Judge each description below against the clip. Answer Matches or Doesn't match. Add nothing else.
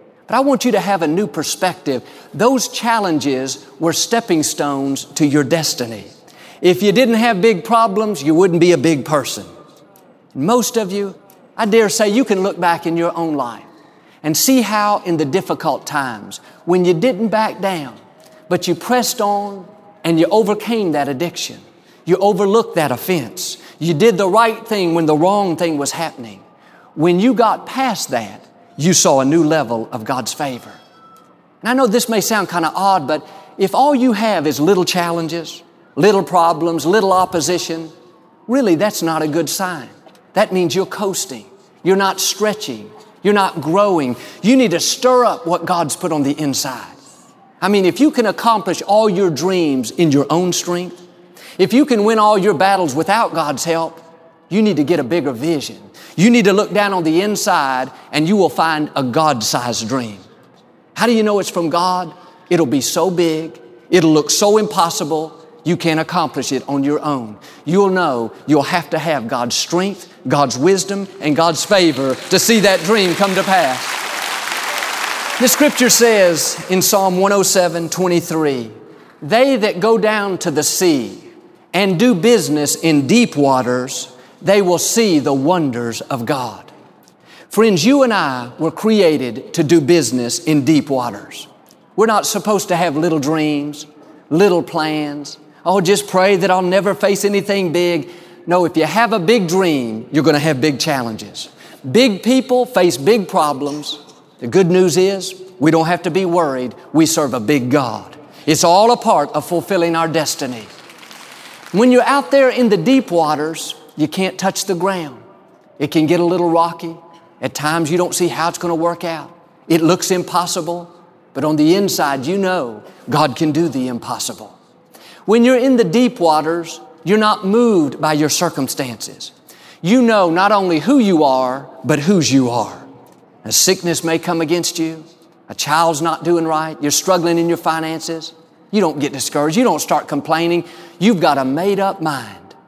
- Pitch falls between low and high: Matches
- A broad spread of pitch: Doesn't match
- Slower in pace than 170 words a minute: Doesn't match